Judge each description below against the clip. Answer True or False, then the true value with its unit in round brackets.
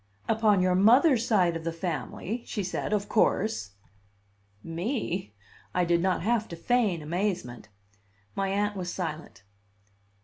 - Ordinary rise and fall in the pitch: True (4.1 semitones)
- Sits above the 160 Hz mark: True (185 Hz)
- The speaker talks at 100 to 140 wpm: True (135 wpm)